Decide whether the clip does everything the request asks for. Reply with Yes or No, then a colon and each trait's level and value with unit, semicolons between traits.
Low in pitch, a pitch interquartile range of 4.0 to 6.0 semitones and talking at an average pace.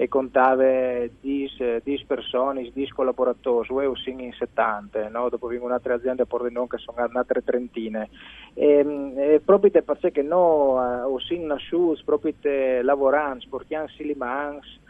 No: low, 130 Hz; average, 2.8 semitones; average, 145 wpm